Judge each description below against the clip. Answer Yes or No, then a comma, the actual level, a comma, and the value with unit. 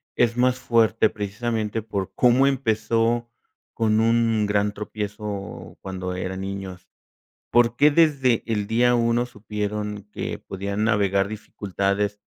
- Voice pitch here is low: Yes, low, 105 Hz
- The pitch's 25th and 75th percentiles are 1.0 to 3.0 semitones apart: Yes, narrow, 2.6 semitones